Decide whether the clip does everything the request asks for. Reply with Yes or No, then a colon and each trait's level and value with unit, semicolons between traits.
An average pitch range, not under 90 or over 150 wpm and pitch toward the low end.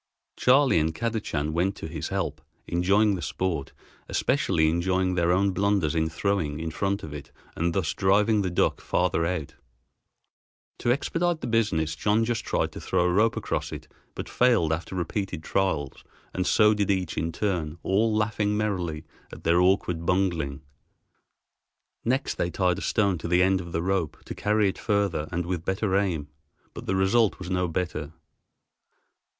No: average, 3.9 semitones; average, 170 wpm; very low, 95 Hz